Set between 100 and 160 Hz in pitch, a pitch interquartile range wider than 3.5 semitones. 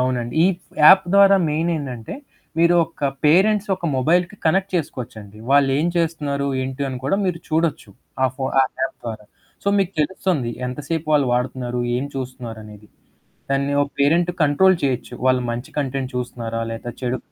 Yes: medium, 140 Hz; average, 5.1 semitones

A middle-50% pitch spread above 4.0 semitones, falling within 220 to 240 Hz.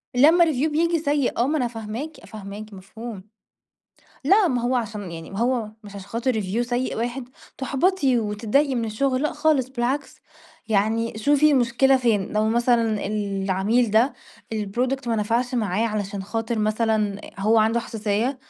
No: average, 3.7 semitones; high, 230 Hz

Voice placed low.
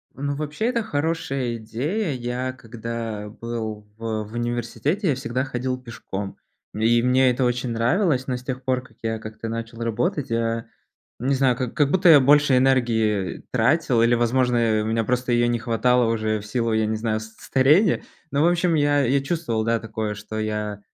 Yes: low, 120 Hz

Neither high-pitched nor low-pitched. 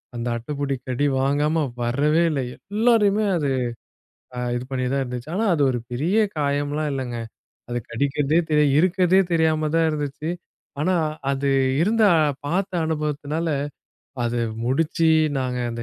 Yes: medium, 150 Hz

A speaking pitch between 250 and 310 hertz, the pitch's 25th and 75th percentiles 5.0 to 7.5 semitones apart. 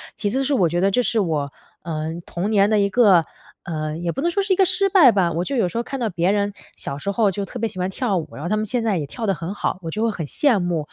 No: high, 200 Hz; wide, 5.4 semitones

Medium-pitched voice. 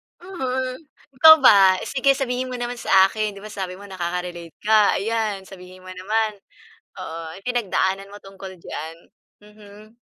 No: high, 205 Hz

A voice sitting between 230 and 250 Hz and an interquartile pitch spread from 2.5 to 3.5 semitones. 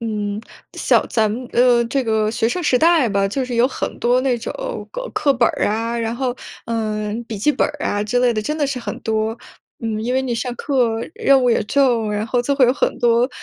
Yes: high, 235 Hz; average, 2.8 semitones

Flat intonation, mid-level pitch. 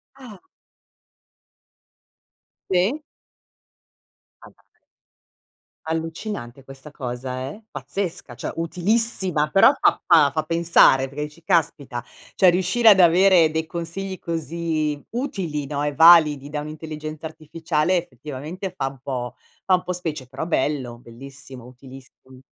No: average, 4.4 semitones; medium, 155 Hz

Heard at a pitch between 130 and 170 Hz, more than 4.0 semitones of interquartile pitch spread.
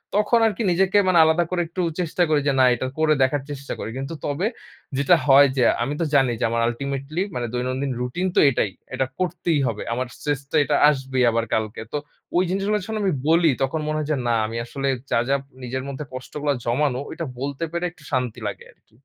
Yes: medium, 140 Hz; average, 4.8 semitones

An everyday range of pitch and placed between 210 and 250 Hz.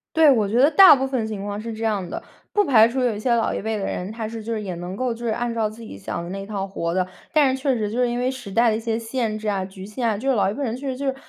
Yes: average, 3.4 semitones; high, 225 Hz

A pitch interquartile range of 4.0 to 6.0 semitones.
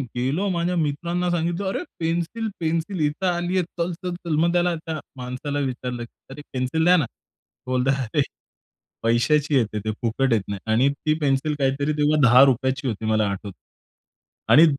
Yes: average, 5.1 semitones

